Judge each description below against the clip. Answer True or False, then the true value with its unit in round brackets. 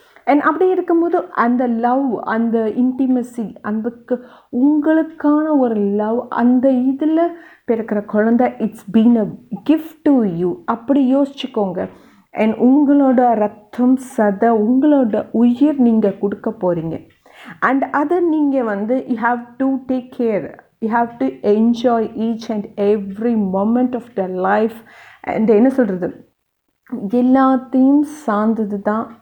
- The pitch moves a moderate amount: True (3.6 semitones)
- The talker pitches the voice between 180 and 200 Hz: False (240 Hz)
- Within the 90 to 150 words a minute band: True (120 wpm)